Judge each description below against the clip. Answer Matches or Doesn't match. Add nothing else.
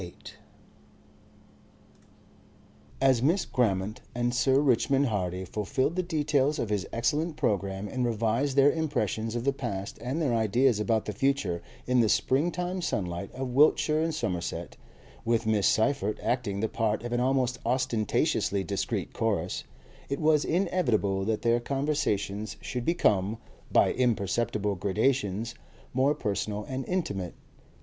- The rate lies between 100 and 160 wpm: Matches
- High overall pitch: Doesn't match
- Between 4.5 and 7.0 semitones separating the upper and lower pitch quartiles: Matches